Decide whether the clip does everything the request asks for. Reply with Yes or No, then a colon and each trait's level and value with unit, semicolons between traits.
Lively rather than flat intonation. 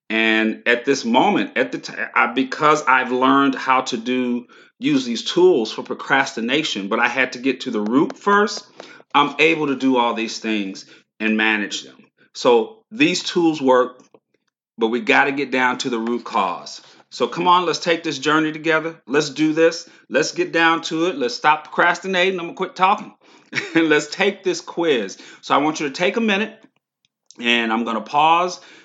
Yes: wide, 5.9 semitones